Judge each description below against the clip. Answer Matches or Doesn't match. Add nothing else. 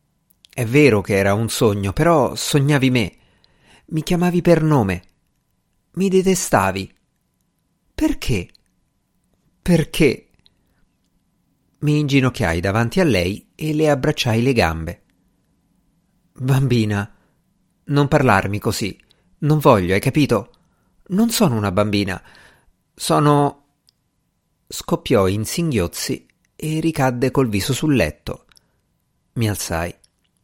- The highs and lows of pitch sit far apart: Matches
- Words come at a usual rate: Doesn't match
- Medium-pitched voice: Doesn't match